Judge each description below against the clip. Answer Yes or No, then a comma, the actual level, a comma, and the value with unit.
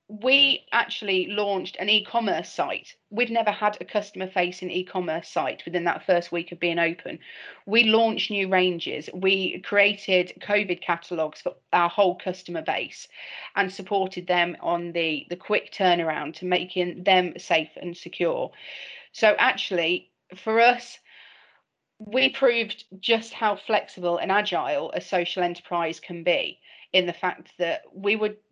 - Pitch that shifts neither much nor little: Yes, average, 3.2 semitones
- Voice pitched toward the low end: No, medium, 185 Hz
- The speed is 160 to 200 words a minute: No, average, 145 wpm